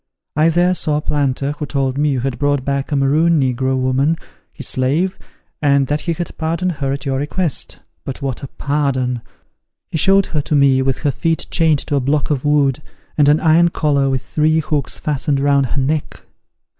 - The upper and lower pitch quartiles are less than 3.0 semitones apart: Yes, narrow, 2.4 semitones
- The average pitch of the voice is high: No, medium, 145 Hz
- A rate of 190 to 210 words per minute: Yes, average, 200 wpm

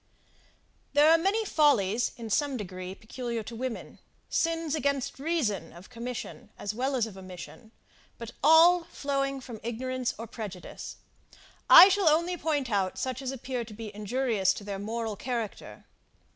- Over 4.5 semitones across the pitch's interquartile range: Yes, average, 5.2 semitones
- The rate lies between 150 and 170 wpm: Yes, average, 155 wpm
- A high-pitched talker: Yes, high, 245 Hz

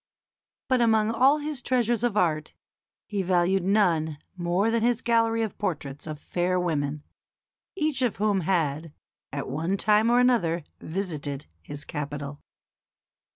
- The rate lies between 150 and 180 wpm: No, average, 140 wpm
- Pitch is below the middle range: No, high, 190 Hz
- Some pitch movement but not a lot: No, wide, 6.6 semitones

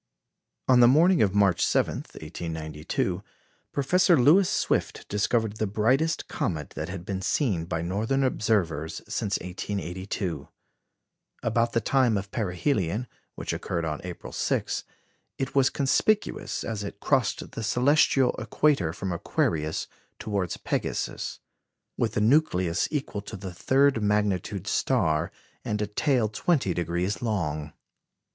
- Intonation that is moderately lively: No, wide, 6.3 semitones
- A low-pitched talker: Yes, low, 105 Hz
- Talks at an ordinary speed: No, slow, 130 wpm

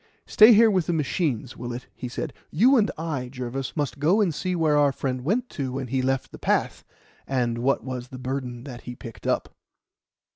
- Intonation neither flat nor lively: Yes, average, 4.6 semitones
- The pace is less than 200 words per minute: No, fast, 205 wpm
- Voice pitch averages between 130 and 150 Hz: Yes, low, 135 Hz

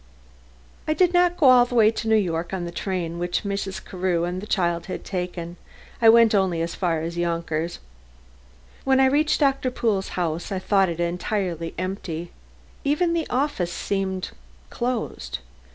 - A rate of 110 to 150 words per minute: No, average, 170 wpm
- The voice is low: No, high, 190 Hz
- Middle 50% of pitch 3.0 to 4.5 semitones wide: No, wide, 5.6 semitones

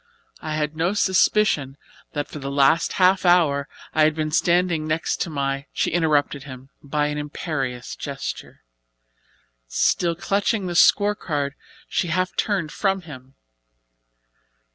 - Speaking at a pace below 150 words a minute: Yes, average, 140 wpm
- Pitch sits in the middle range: Yes, medium, 155 Hz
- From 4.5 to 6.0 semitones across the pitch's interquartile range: No, average, 4.0 semitones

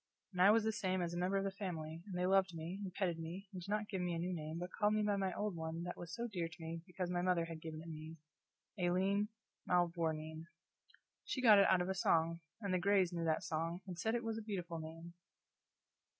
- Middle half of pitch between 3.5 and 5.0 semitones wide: No, average, 2.8 semitones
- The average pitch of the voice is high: No, medium, 180 Hz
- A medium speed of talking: No, fast, 250 wpm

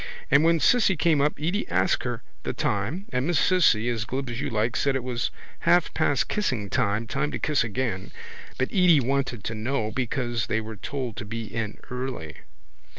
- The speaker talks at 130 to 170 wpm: No, average, 195 wpm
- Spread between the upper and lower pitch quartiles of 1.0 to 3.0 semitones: No, average, 4.8 semitones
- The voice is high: No, low, 125 Hz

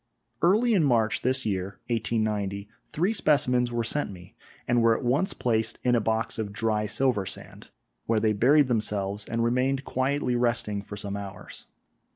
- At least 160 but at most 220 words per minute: Yes, average, 170 wpm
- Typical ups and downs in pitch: Yes, average, 3.6 semitones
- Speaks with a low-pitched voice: Yes, low, 115 Hz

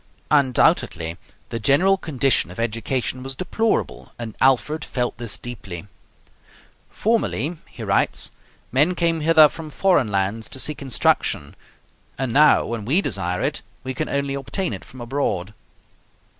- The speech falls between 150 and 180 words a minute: No, average, 140 wpm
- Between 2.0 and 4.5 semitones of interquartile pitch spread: No, average, 5.0 semitones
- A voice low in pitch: Yes, low, 130 Hz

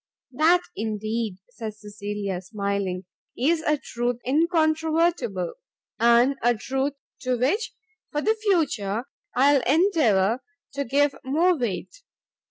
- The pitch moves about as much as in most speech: No, wide, 6.7 semitones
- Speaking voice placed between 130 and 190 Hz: No, very high, 255 Hz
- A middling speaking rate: No, slow, 115 wpm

